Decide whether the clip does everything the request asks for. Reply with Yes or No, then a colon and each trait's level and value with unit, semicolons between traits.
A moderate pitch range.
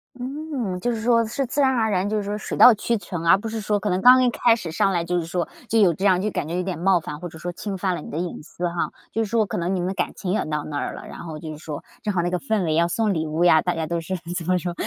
Yes: average, 4.2 semitones